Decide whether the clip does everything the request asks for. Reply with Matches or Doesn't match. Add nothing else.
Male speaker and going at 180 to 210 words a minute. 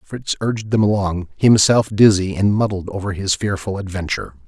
Doesn't match